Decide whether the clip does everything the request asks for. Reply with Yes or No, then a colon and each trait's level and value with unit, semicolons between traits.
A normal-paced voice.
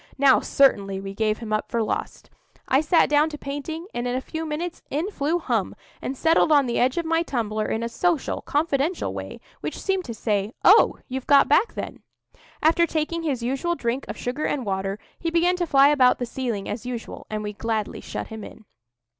No: fast, 210 wpm